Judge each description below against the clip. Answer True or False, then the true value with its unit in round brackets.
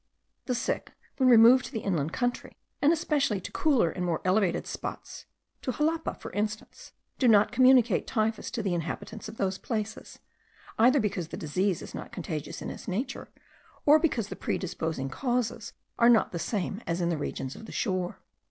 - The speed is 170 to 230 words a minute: True (180 wpm)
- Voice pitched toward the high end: True (215 Hz)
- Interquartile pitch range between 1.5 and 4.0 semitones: False (5.6 semitones)